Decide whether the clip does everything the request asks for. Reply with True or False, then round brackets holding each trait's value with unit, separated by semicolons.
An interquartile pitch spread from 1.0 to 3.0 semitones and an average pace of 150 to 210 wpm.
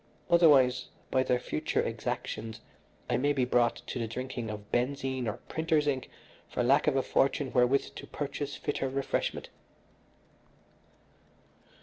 False (2.5 semitones; 135 wpm)